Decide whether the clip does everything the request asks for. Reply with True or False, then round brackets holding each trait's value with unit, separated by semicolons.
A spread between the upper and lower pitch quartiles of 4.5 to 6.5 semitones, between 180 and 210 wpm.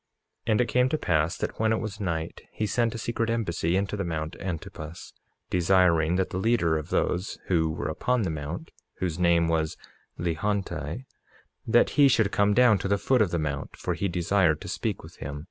True (4.8 semitones; 205 wpm)